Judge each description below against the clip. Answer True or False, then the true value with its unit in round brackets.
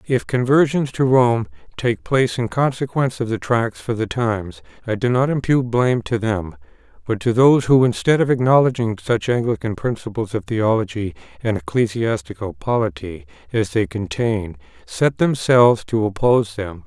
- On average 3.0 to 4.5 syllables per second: False (5.1 syllables/s)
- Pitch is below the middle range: True (120 Hz)